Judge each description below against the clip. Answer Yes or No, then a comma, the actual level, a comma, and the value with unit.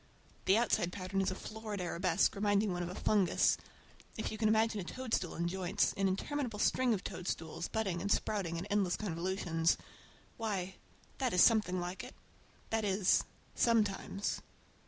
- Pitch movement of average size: Yes, average, 3.2 semitones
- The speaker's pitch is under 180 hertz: No, high, 195 Hz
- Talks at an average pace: Yes, average, 155 wpm